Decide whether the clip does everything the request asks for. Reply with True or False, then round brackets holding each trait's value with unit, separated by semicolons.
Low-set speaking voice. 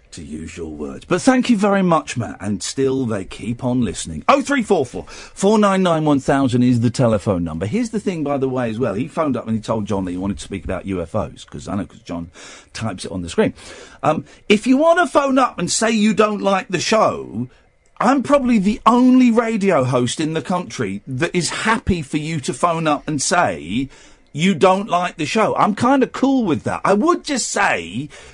False (170 Hz)